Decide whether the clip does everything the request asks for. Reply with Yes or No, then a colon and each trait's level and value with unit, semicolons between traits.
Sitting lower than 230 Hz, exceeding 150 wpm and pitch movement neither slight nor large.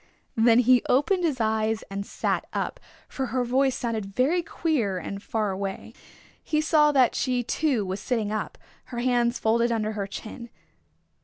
No: high, 235 Hz; average, 165 wpm; average, 3.4 semitones